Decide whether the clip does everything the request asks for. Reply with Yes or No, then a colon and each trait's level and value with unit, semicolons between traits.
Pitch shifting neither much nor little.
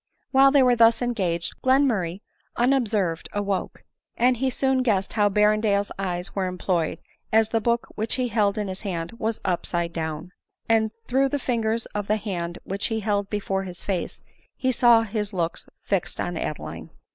Yes: average, 3.8 semitones